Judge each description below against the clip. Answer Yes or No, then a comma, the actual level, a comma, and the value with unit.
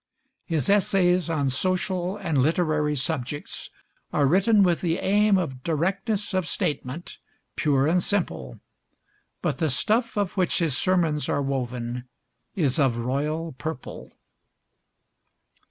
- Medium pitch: Yes, medium, 160 Hz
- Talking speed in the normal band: No, slow, 120 wpm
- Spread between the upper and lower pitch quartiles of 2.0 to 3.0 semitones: No, average, 5.2 semitones